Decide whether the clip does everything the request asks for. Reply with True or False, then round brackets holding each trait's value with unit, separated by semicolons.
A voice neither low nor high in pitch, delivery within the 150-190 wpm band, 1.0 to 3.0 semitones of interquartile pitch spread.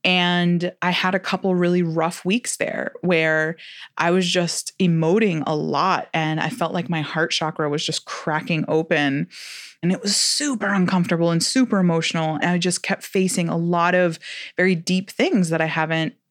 True (175 Hz; 180 wpm; 2.4 semitones)